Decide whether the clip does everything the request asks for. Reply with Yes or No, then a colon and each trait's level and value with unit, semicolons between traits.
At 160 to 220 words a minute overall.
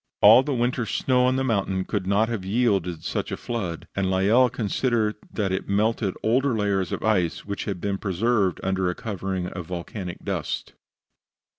Yes: average, 175 wpm